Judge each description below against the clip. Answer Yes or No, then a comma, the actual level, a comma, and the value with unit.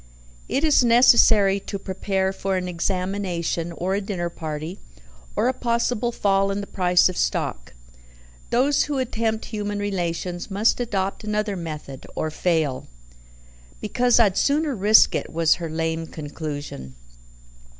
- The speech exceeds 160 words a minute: No, average, 140 wpm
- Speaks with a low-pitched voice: No, high, 195 Hz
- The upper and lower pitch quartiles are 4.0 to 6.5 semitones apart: Yes, average, 4.4 semitones